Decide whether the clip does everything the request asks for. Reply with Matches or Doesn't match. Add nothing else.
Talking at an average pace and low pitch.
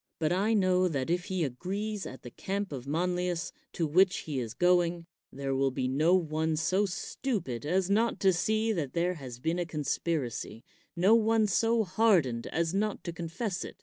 Doesn't match